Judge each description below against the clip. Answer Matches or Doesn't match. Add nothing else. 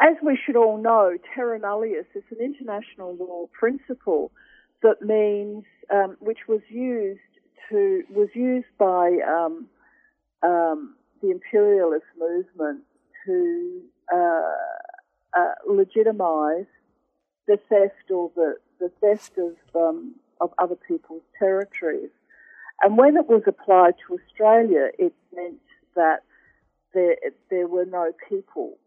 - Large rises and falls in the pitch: Matches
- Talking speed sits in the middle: Doesn't match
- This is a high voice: Matches